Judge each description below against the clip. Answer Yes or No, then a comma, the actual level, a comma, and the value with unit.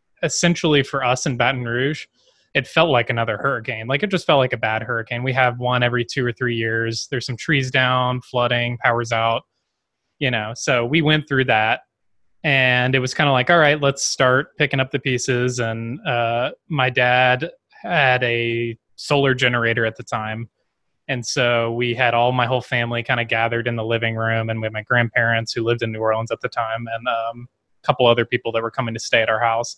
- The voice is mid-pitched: No, low, 125 Hz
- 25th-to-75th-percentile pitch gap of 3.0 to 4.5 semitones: No, narrow, 2.4 semitones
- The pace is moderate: No, fast, 220 wpm